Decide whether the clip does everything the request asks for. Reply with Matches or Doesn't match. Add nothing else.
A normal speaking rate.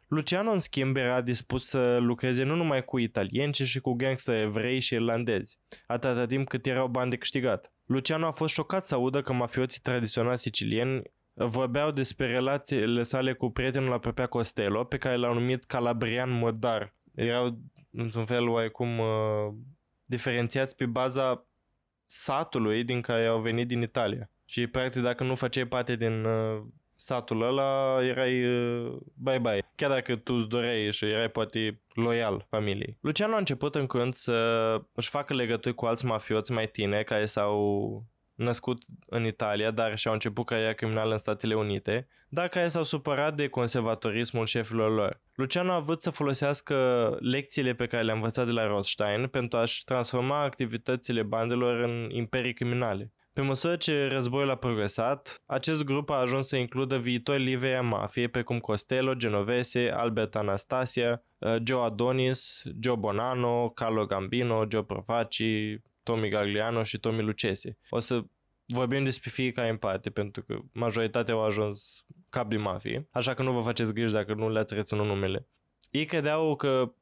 Matches